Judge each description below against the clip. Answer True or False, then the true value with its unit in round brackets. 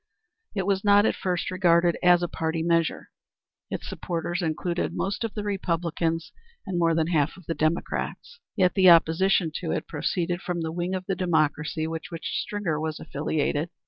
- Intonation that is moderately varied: False (2.3 semitones)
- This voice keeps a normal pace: True (175 wpm)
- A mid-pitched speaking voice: True (170 Hz)